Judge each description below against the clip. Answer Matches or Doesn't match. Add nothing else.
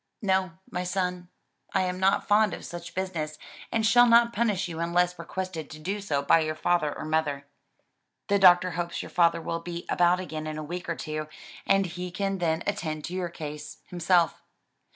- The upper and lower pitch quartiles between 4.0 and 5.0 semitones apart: Doesn't match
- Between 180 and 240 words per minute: Matches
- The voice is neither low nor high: Matches